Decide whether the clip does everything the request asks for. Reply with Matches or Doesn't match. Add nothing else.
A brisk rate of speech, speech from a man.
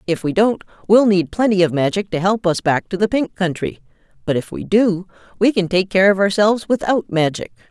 Doesn't match